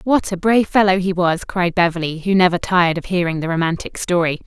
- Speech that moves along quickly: Yes, fast, 215 wpm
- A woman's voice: Yes, female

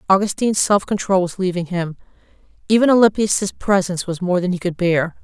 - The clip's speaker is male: No, female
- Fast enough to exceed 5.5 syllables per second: Yes, 5.8 syllables/s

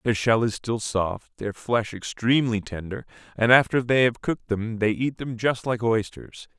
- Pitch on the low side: Yes, low, 115 Hz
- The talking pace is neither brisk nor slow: Yes, average, 190 wpm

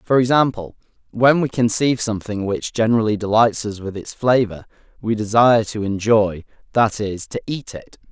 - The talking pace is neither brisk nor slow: Yes, average, 165 wpm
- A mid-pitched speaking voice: No, low, 110 Hz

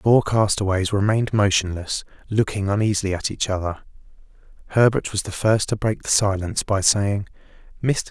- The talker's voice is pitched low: Yes, low, 100 Hz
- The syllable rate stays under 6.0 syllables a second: Yes, 5.5 syllables/s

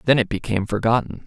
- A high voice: No, low, 115 Hz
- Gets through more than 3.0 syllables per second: Yes, 7.1 syllables/s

